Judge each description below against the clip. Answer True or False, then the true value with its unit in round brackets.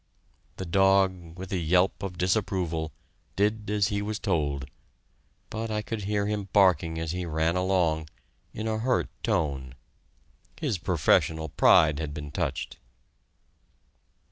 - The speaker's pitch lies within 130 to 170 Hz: False (90 Hz)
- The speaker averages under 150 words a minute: True (135 wpm)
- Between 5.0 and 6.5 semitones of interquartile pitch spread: False (4.2 semitones)